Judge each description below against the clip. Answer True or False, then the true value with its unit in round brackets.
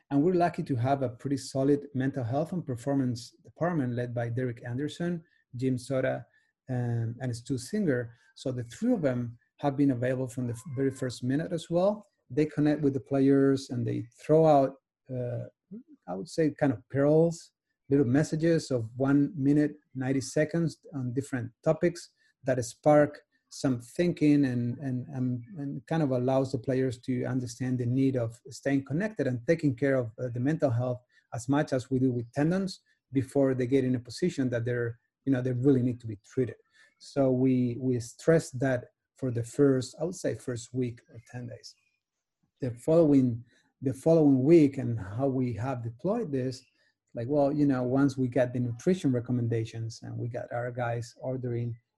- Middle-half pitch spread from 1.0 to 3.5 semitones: True (2.9 semitones)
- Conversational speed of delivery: True (180 wpm)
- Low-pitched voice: True (130 Hz)